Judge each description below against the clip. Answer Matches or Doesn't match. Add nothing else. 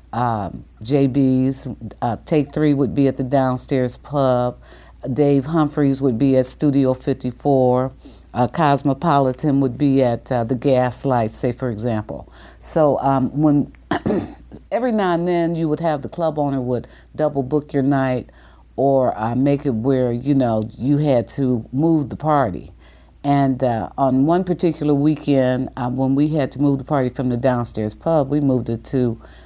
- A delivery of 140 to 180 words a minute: Matches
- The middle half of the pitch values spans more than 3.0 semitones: Doesn't match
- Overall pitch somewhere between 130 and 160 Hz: Matches